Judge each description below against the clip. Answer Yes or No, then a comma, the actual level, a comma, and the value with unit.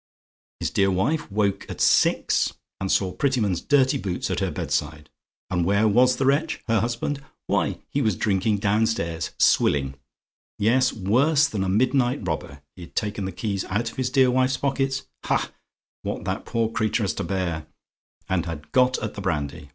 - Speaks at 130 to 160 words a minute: No, average, 175 wpm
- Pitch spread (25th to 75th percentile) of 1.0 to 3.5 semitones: No, wide, 5.5 semitones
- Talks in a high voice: No, low, 110 Hz